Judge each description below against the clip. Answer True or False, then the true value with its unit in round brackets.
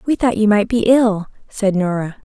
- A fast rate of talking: True (210 wpm)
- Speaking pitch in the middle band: False (210 Hz)